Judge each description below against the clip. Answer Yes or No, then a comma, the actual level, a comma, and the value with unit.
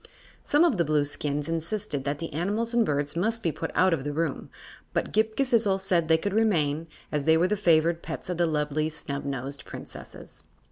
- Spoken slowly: No, average, 195 wpm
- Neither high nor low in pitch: Yes, medium, 165 Hz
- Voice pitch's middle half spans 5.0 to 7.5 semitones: Yes, wide, 5.5 semitones